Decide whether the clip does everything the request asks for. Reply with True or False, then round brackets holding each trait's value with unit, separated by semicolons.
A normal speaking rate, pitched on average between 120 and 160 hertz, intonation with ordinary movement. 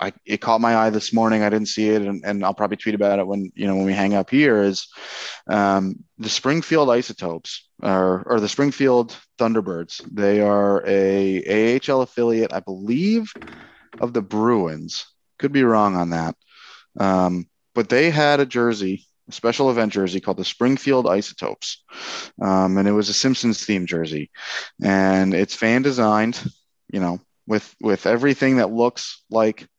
False (170 wpm; 105 Hz; 3.7 semitones)